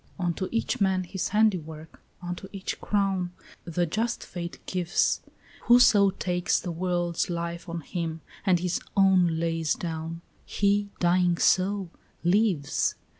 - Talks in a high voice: No, medium, 180 Hz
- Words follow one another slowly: Yes, slow, 130 wpm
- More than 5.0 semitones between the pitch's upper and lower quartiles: No, narrow, 2.4 semitones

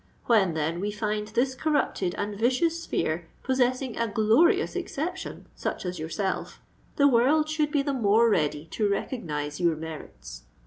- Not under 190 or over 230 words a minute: No, average, 150 wpm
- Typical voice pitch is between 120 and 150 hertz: No, high, 220 Hz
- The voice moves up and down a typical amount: No, wide, 7.5 semitones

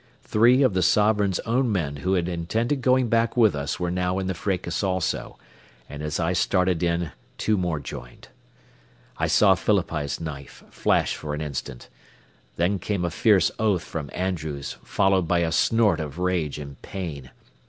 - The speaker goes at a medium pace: Yes, average, 170 wpm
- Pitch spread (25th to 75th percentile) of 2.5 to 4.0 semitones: No, average, 4.4 semitones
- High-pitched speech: No, very low, 90 Hz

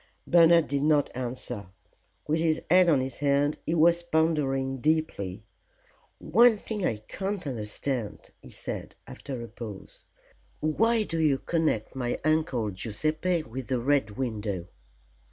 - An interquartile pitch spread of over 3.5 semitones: Yes, average, 5.2 semitones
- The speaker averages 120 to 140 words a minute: Yes, slow, 135 wpm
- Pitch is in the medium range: Yes, medium, 145 Hz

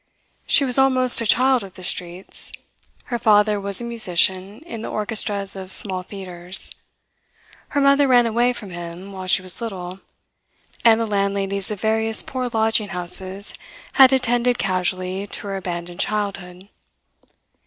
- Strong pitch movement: No, average, 4.0 semitones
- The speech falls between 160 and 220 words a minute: No, average, 150 wpm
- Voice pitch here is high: Yes, high, 200 Hz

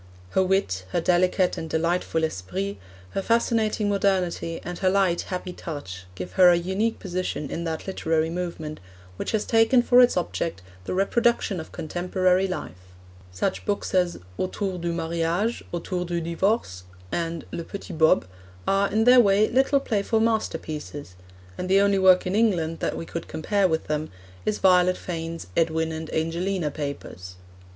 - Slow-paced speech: No, average, 160 wpm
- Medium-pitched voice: Yes, medium, 180 Hz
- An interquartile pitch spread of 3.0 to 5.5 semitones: Yes, average, 3.4 semitones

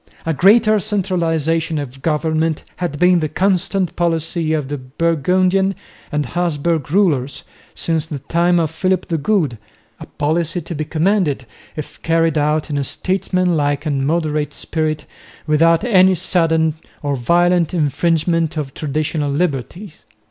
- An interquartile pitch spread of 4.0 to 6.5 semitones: No, average, 3.0 semitones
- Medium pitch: Yes, medium, 165 Hz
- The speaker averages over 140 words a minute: No, slow, 135 wpm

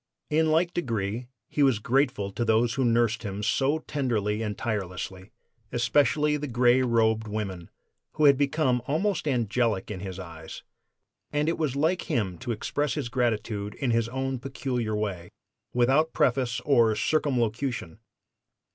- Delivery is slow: No, average, 145 wpm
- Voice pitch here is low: Yes, low, 120 Hz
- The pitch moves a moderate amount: Yes, average, 4.6 semitones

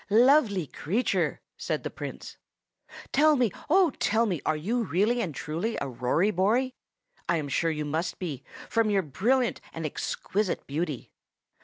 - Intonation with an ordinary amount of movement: No, wide, 7.1 semitones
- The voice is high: Yes, high, 195 Hz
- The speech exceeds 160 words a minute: No, average, 155 wpm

